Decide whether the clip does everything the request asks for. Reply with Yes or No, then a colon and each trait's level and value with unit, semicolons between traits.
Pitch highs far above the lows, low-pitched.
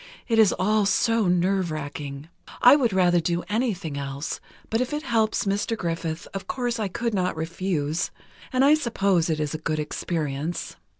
No: wide, 5.9 semitones; medium, 185 Hz